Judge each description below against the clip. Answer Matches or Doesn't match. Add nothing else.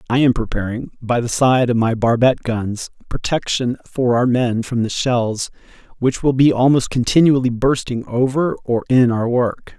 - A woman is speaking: Doesn't match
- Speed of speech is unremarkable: Matches